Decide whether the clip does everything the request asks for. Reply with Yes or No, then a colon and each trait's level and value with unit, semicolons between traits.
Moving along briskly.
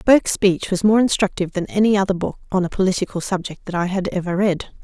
Yes: fast, 225 wpm